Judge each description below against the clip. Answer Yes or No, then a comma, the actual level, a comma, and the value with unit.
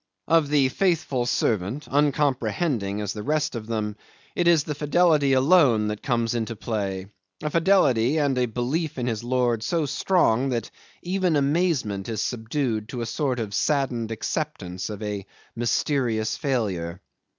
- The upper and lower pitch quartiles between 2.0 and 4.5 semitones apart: No, average, 5.3 semitones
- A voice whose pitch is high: No, low, 125 Hz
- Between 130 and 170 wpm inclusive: Yes, average, 150 wpm